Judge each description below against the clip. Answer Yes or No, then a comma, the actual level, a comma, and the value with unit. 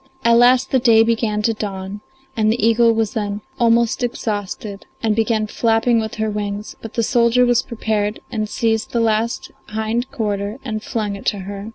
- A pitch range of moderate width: No, narrow, 1.8 semitones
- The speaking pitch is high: Yes, high, 220 Hz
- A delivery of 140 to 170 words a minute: No, average, 185 wpm